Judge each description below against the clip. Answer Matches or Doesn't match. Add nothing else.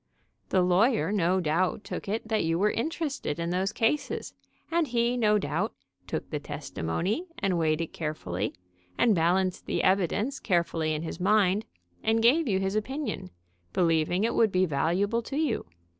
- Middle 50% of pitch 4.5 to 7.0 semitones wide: Matches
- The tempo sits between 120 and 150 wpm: Doesn't match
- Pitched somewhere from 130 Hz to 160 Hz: Doesn't match